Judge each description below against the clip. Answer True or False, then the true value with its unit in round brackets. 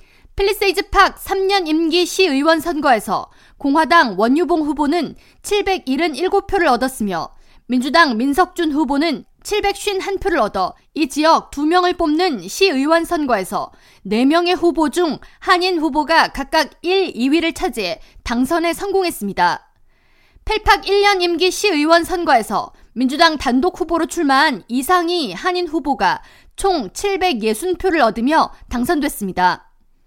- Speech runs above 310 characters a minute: False (255 characters per minute)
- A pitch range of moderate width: True (4.3 semitones)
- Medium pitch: False (335 Hz)